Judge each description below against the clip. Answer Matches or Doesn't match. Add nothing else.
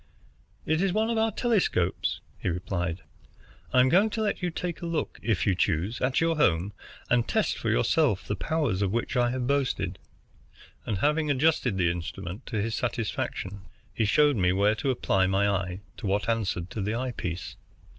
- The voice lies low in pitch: Matches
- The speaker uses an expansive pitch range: Matches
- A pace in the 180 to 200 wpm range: Matches